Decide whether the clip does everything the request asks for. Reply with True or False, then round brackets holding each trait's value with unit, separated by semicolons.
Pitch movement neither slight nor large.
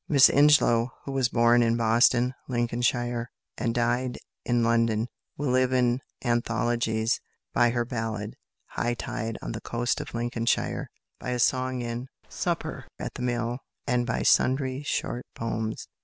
False (1.3 semitones)